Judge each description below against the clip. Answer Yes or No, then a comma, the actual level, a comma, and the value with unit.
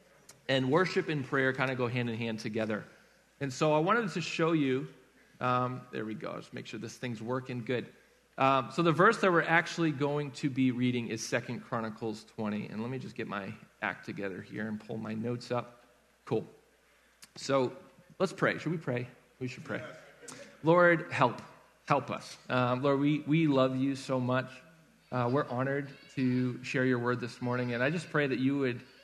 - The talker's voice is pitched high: No, low, 130 Hz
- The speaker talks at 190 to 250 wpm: Yes, average, 200 wpm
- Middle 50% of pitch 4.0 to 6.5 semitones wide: No, average, 3.3 semitones